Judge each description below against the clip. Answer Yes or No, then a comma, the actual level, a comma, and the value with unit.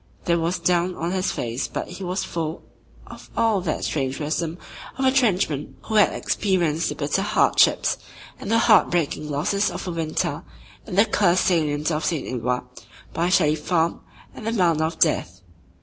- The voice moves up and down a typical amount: Yes, average, 3.7 semitones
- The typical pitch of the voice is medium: Yes, medium, 170 Hz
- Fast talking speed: No, average, 175 wpm